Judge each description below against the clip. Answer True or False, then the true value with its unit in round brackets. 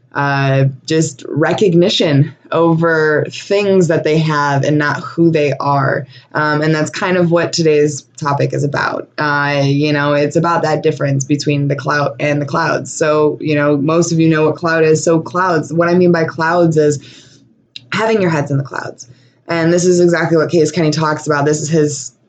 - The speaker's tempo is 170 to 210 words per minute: True (195 wpm)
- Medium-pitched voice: True (150 Hz)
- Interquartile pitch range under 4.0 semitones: True (2.4 semitones)